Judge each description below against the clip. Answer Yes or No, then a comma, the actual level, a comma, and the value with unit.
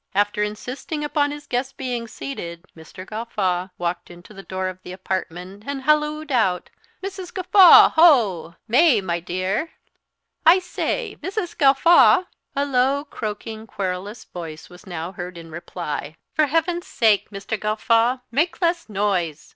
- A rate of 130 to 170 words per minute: Yes, average, 145 wpm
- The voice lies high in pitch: Yes, high, 215 Hz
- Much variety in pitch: Yes, wide, 7.9 semitones